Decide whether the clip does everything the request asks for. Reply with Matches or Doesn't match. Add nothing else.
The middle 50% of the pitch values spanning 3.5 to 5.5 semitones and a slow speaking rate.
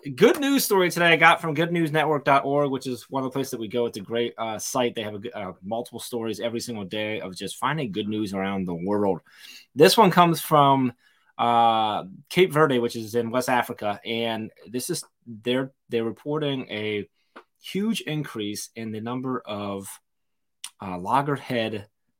Doesn't match